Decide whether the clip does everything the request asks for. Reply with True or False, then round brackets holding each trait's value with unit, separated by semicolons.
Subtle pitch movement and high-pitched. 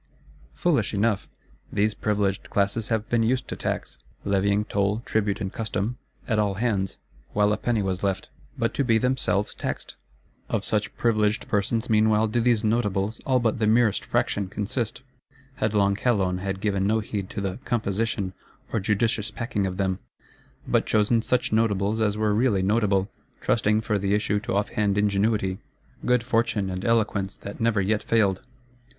False (2.3 semitones; 105 Hz)